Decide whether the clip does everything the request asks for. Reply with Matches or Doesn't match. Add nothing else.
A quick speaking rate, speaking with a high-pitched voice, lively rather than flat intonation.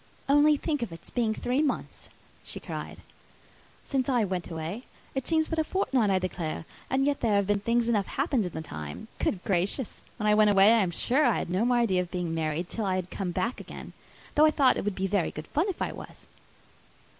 Matches